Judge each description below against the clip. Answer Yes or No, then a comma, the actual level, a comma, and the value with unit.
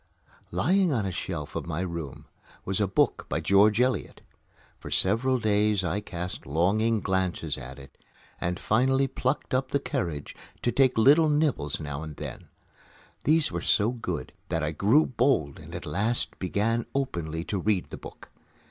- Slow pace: No, average, 165 wpm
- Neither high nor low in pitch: No, low, 100 Hz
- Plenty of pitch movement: Yes, wide, 7.0 semitones